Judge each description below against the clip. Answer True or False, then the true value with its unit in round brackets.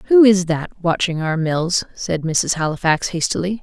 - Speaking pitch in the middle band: True (175 Hz)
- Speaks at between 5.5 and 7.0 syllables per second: False (4.3 syllables/s)